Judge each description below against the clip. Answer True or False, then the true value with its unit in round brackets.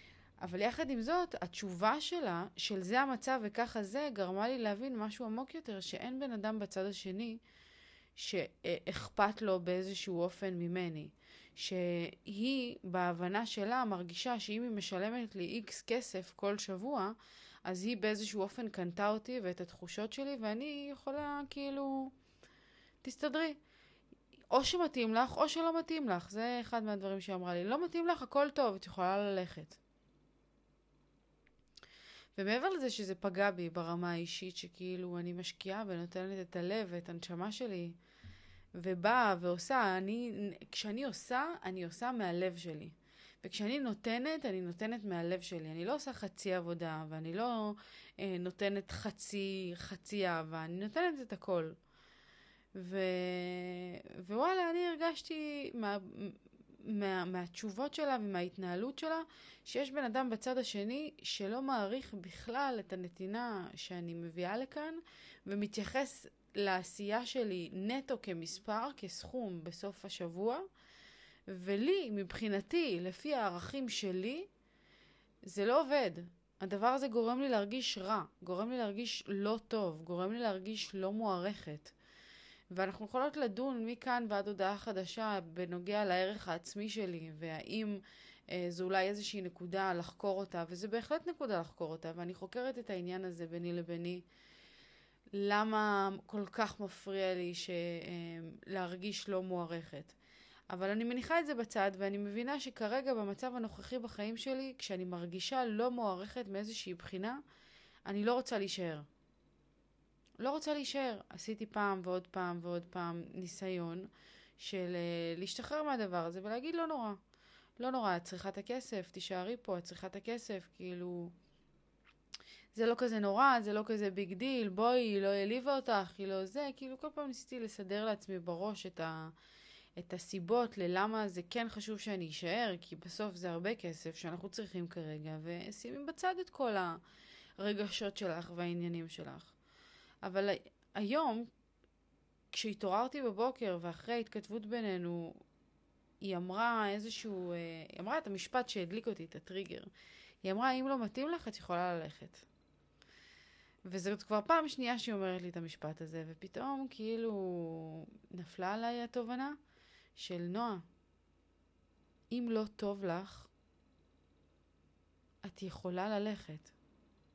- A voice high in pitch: True (200 Hz)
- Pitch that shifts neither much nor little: True (4.8 semitones)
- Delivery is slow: False (130 wpm)